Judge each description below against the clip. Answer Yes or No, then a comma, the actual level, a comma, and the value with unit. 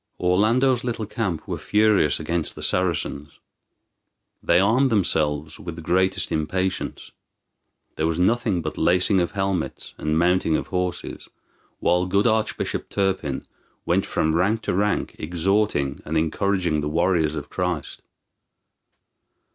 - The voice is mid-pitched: No, very low, 90 Hz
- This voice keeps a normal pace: No, slow, 130 wpm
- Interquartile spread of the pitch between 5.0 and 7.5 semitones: No, average, 4.0 semitones